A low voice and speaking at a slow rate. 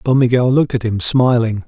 No: low, 120 Hz; fast, 215 wpm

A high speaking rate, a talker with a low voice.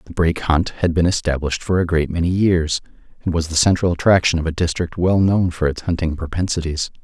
Yes: fast, 215 wpm; very low, 85 Hz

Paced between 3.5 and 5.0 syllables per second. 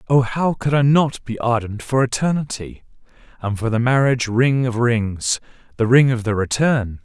Yes: 4.7 syllables/s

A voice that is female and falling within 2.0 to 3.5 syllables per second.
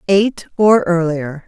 Yes: female; 3.4 syllables/s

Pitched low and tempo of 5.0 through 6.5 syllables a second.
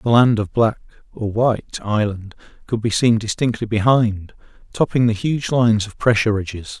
Yes: low, 110 Hz; 5.1 syllables/s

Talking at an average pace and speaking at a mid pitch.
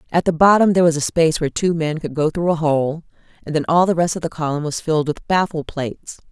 No: fast, 265 wpm; medium, 160 Hz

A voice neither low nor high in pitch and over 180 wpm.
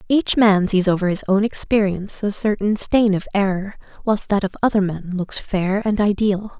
No: high, 200 Hz; average, 190 wpm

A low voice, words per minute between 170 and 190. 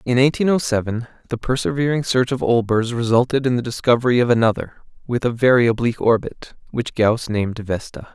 Yes: low, 120 Hz; average, 175 wpm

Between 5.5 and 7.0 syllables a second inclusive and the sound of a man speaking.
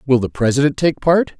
Yes: 5.7 syllables/s; male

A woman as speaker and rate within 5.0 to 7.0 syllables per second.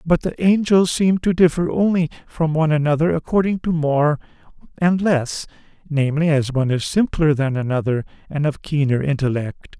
No: male; 5.2 syllables/s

